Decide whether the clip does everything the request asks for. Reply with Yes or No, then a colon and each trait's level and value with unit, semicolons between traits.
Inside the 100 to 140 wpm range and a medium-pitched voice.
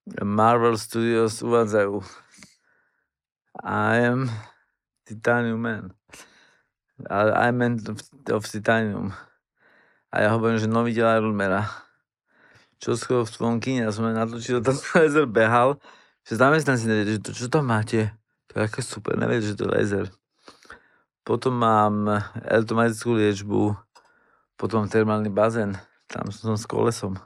No: average, 130 wpm; low, 115 Hz